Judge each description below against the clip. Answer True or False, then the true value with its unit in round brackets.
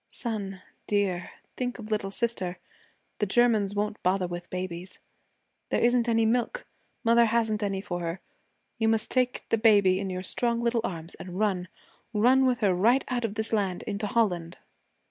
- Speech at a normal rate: True (165 wpm)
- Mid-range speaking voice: False (210 Hz)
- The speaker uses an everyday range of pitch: True (3.9 semitones)